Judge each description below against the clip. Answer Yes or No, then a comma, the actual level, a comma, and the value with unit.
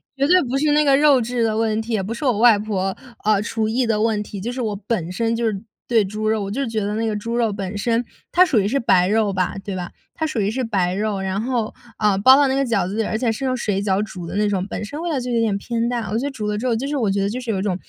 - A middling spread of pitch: Yes, average, 3.2 semitones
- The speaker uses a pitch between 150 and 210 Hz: No, high, 220 Hz